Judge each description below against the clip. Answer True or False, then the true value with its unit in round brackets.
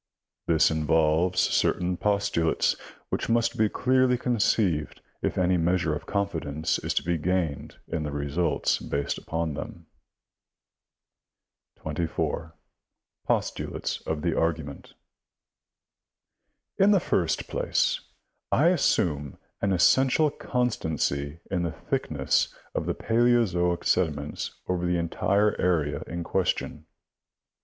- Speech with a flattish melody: False (4.3 semitones)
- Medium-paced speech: False (115 wpm)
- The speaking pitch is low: True (85 Hz)